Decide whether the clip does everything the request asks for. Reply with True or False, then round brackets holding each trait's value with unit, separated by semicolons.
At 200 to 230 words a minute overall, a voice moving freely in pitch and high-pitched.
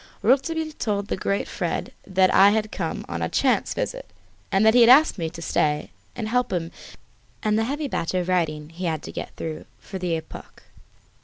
True (205 wpm; 6.3 semitones; 200 Hz)